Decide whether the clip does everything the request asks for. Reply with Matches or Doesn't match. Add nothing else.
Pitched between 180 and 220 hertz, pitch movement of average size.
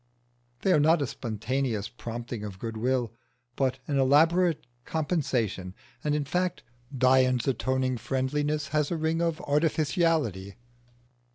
Doesn't match